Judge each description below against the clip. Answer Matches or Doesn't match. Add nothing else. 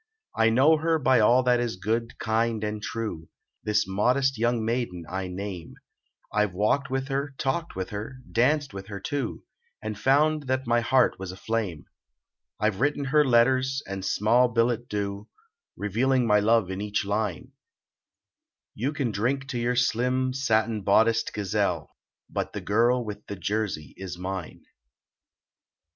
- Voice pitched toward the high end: Doesn't match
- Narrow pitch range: Doesn't match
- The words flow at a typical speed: Matches